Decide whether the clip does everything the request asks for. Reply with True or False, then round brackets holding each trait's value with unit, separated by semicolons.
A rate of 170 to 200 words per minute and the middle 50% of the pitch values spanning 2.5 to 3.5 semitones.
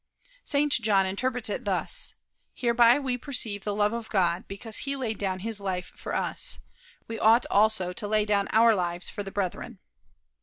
True (180 wpm; 3.2 semitones)